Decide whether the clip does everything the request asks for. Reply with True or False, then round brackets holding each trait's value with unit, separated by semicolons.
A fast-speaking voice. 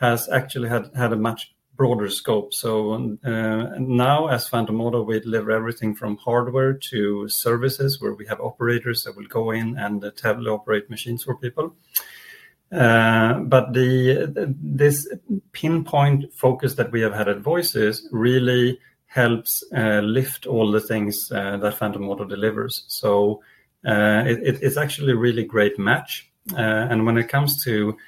False (160 wpm)